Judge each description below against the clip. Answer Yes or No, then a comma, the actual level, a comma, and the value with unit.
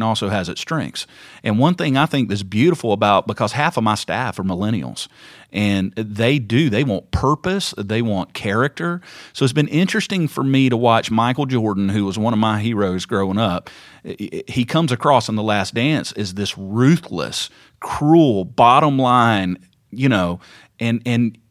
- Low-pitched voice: Yes, low, 115 Hz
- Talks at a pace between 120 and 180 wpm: Yes, average, 175 wpm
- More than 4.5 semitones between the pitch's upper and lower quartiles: Yes, average, 5.1 semitones